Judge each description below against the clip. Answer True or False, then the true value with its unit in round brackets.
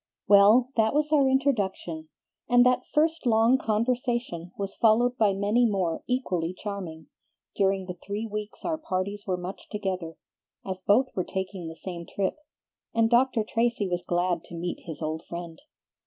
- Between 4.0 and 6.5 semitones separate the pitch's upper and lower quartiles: True (4.9 semitones)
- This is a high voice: True (200 Hz)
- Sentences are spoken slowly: False (160 wpm)